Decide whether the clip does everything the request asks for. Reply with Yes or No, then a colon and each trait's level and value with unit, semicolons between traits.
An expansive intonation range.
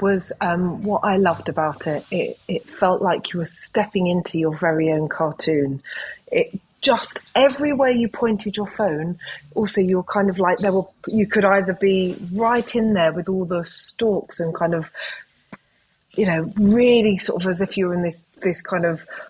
No: average, 3.8 semitones